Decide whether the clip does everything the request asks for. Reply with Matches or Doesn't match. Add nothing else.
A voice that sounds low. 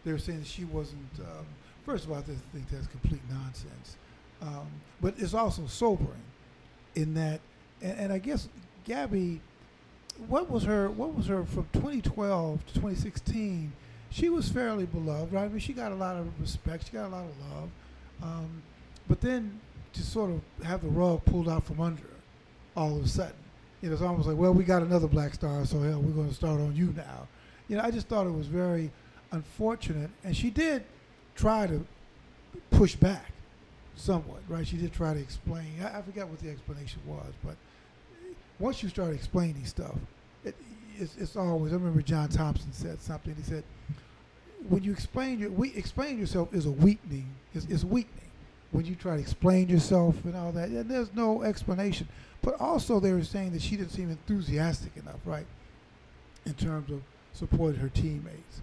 Doesn't match